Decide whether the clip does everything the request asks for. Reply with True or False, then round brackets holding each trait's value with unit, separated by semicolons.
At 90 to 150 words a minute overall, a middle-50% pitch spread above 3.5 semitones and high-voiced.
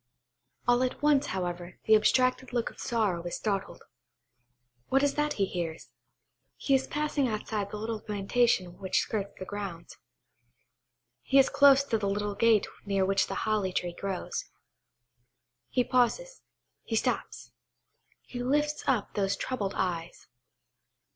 True (140 wpm; 4.9 semitones; 215 Hz)